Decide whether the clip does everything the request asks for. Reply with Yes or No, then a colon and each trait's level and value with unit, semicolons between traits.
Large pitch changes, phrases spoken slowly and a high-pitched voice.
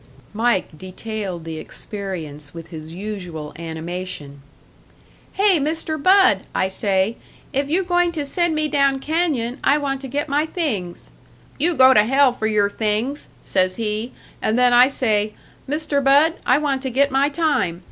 No: wide, 7.4 semitones; average, 160 wpm; high, 245 Hz